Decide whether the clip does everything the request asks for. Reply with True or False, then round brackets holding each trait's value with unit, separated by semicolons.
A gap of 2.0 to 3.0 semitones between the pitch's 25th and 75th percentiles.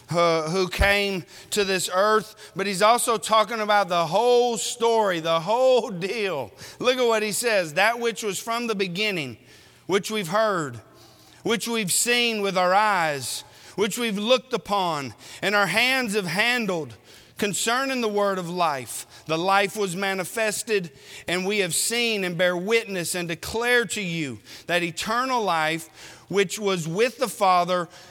False (4.6 semitones)